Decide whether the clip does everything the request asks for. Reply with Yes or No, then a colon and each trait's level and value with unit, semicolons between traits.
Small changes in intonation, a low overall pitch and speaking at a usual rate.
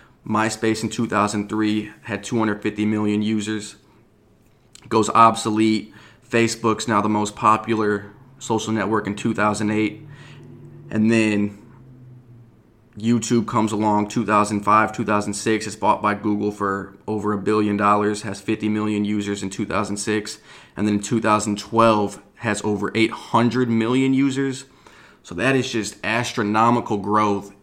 No: narrow, 1.8 semitones; low, 110 Hz; slow, 120 wpm